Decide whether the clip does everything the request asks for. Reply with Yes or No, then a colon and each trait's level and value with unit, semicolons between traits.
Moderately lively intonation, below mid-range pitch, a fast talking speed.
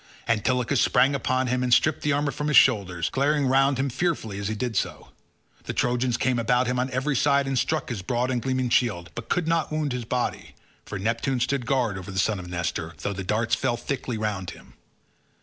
Yes: average, 3.7 semitones; low, 125 Hz; fast, 220 wpm